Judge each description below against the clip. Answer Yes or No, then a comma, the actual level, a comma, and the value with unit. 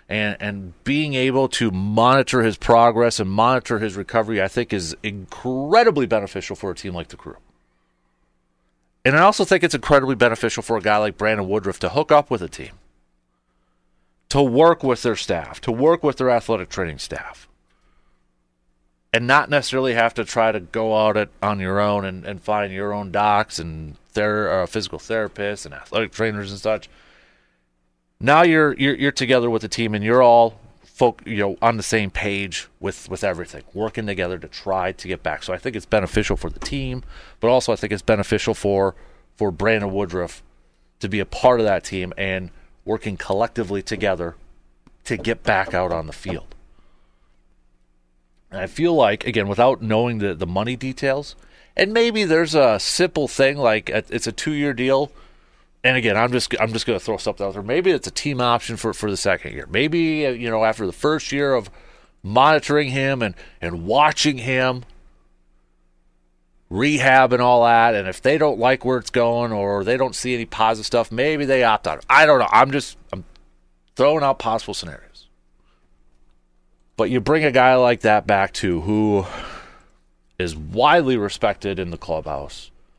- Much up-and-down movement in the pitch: Yes, wide, 7.0 semitones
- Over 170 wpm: Yes, average, 185 wpm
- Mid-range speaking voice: No, low, 105 Hz